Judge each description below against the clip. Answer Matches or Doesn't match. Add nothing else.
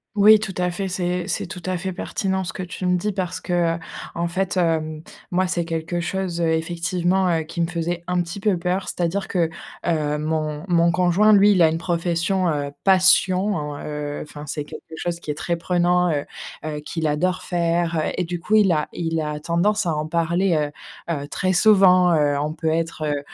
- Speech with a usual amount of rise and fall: Doesn't match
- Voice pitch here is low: Doesn't match